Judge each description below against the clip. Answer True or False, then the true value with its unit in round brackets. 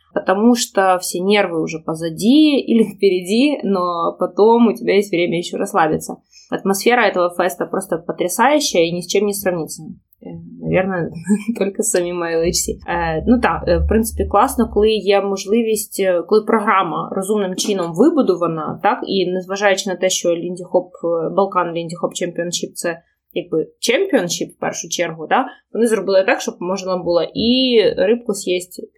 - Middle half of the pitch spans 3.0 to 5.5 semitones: True (4.1 semitones)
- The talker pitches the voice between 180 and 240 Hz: True (190 Hz)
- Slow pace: False (145 wpm)